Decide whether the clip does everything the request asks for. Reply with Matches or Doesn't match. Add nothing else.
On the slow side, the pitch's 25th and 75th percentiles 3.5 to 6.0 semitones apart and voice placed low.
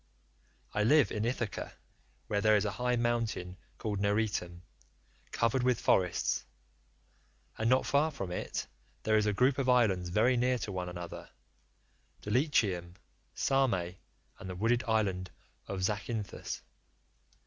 Matches